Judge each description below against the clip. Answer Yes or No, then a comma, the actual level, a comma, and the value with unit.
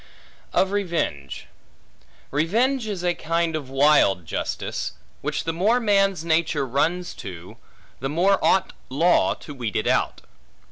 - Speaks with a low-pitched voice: No, medium, 165 Hz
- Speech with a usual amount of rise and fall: No, wide, 5.8 semitones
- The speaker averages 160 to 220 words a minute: No, slow, 135 wpm